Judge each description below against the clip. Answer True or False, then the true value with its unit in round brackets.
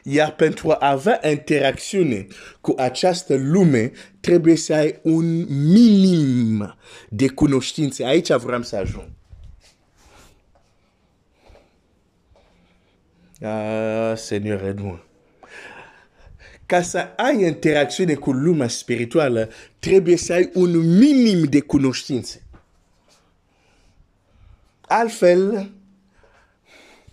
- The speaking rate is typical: False (90 wpm)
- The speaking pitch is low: True (130 Hz)